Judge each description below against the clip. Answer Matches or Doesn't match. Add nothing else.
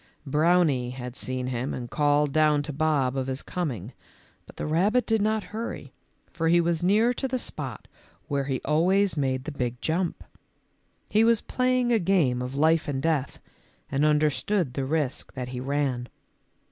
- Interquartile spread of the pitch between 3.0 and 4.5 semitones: Doesn't match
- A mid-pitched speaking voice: Matches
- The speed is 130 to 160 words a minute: Doesn't match